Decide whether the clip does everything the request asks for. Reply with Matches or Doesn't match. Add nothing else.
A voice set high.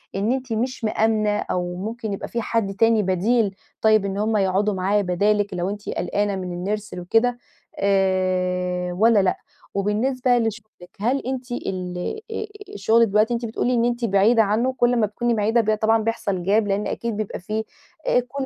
Matches